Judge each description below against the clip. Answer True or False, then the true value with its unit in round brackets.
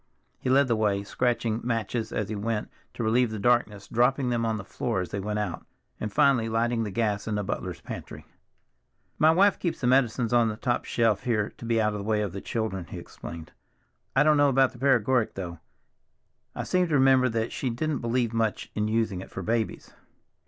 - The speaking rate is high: True (215 wpm)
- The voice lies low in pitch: True (115 Hz)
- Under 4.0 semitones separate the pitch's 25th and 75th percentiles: True (2.9 semitones)